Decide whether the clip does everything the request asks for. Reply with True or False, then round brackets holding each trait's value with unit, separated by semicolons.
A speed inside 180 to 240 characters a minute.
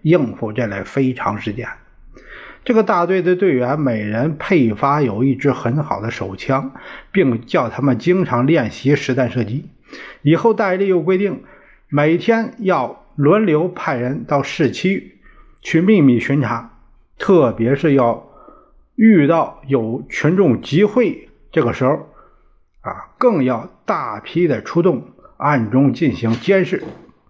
True (200 characters per minute)